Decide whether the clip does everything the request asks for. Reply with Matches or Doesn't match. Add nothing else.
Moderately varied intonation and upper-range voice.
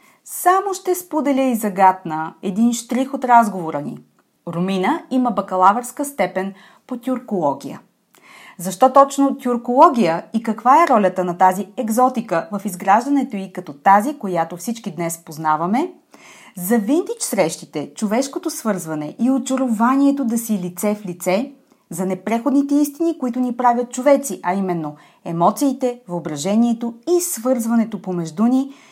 Doesn't match